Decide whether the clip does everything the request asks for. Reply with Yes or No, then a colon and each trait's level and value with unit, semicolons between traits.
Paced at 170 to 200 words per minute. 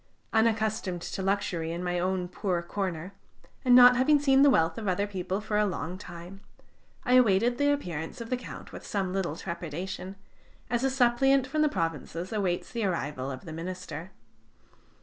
Yes: average, 175 wpm